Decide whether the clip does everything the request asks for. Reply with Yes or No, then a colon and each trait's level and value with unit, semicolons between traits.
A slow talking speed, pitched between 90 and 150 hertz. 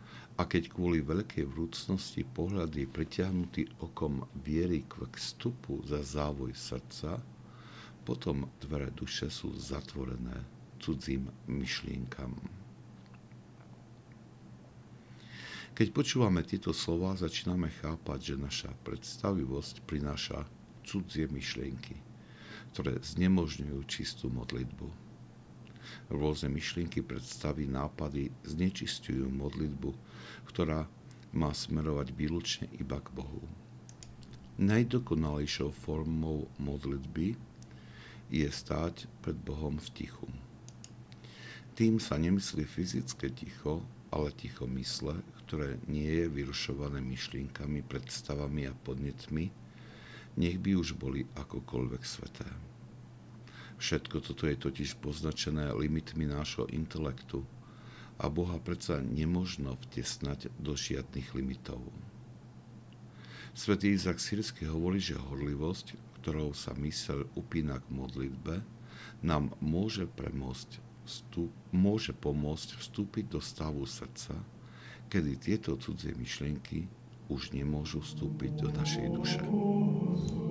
No: slow, 95 wpm; very low, 75 Hz